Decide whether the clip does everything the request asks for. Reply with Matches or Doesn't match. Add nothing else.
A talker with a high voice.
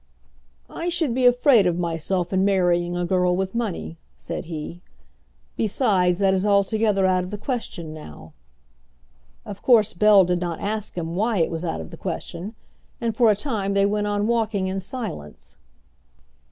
Matches